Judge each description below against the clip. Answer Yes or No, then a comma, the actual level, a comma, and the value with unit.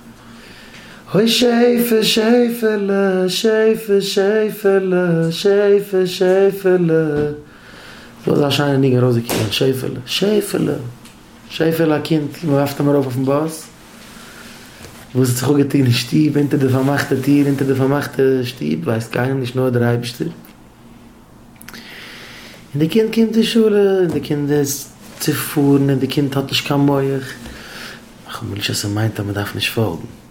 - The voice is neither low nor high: Yes, medium, 145 Hz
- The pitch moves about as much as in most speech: No, wide, 6.3 semitones